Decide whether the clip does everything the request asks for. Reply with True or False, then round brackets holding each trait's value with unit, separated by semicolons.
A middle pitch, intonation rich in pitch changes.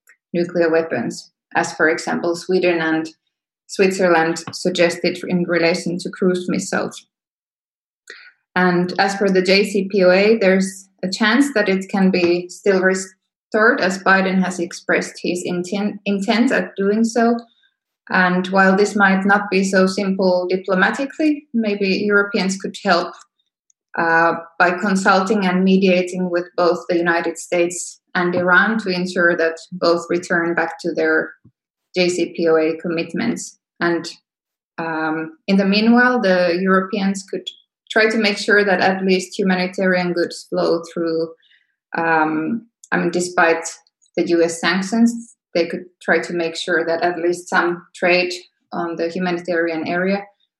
False (180 Hz; 2.5 semitones)